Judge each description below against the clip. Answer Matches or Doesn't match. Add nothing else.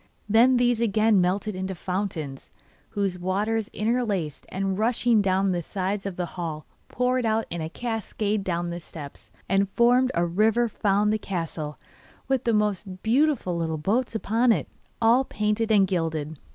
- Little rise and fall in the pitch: Doesn't match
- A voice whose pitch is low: Doesn't match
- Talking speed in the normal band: Matches